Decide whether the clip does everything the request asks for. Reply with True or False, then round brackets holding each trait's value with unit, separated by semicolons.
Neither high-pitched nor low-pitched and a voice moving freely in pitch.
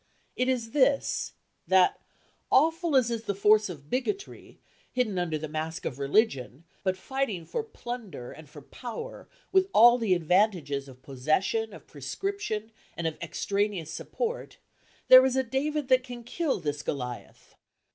False (215 Hz; 8.3 semitones)